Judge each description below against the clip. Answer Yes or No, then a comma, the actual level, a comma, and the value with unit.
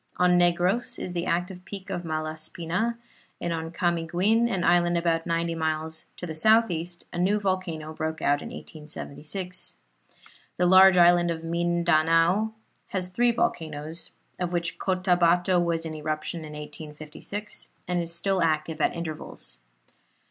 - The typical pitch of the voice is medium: Yes, medium, 170 Hz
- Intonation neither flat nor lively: No, narrow, 2.2 semitones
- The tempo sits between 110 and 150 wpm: Yes, average, 140 wpm